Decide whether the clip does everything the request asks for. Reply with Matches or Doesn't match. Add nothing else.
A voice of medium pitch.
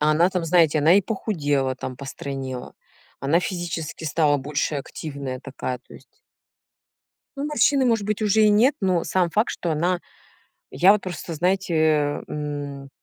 Matches